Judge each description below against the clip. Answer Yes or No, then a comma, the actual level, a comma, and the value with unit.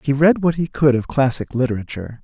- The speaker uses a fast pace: Yes, fast, 215 wpm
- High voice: No, medium, 140 Hz